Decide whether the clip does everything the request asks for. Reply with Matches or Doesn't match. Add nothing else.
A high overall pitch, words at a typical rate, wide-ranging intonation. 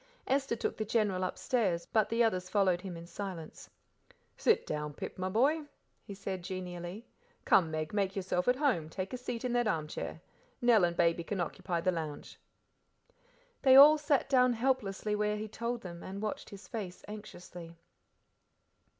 Doesn't match